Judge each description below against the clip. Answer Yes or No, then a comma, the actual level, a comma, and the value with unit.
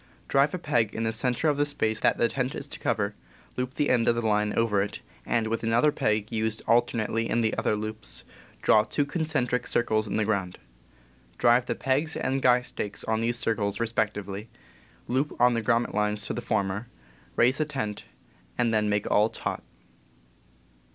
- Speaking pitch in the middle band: No, low, 115 Hz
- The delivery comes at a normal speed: Yes, average, 190 wpm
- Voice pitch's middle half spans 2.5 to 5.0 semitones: Yes, average, 2.8 semitones